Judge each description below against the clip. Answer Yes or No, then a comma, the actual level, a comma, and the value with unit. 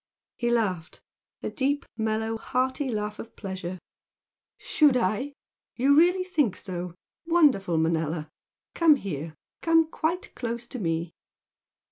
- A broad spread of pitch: Yes, wide, 7.8 semitones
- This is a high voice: Yes, high, 225 Hz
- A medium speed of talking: No, slow, 120 wpm